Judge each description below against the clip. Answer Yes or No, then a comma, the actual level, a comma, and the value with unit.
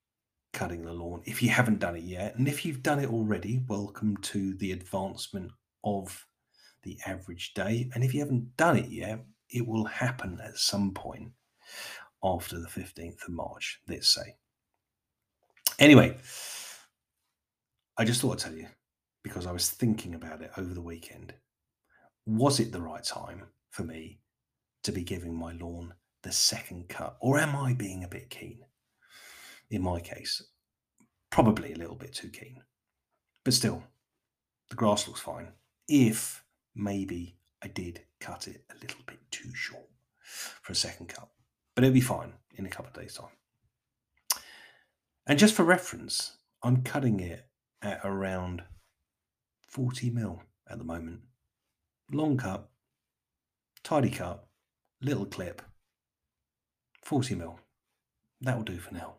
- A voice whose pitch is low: Yes, low, 105 Hz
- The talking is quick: No, average, 150 wpm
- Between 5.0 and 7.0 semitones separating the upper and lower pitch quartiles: Yes, wide, 5.4 semitones